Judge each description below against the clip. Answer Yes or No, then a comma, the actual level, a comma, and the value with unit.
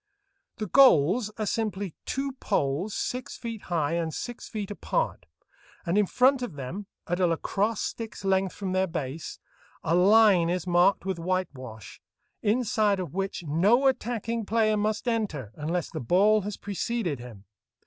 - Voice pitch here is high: Yes, high, 195 Hz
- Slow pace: No, average, 155 wpm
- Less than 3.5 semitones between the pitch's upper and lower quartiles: No, average, 4.6 semitones